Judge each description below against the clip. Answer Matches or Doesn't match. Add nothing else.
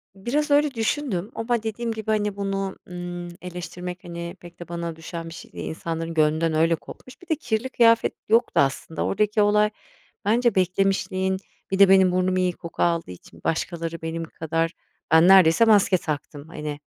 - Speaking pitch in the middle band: Matches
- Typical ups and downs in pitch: Matches